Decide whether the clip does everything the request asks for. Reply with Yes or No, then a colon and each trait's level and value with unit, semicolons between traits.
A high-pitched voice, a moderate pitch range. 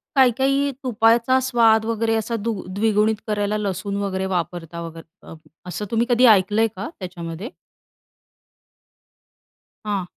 Yes: high, 215 Hz; average, 3.6 semitones